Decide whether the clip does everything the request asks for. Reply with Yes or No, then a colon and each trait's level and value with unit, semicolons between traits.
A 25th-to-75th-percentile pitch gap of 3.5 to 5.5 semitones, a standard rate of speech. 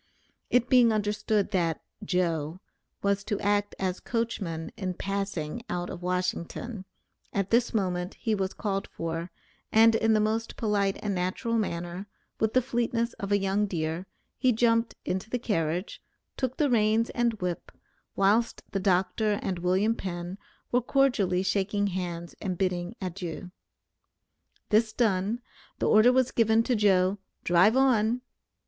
Yes: average, 3.8 semitones; average, 145 wpm